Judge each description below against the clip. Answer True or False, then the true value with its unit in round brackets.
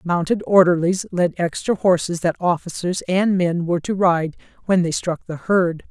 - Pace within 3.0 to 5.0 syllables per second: True (4.7 syllables/s)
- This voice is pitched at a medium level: True (175 Hz)